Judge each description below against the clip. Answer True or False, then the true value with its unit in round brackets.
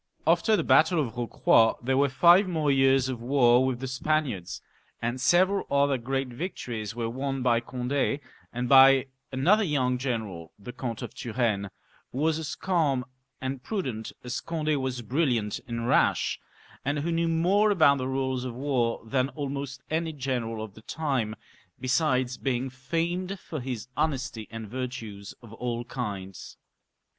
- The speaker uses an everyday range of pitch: True (3.5 semitones)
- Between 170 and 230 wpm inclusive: False (160 wpm)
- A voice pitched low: True (130 Hz)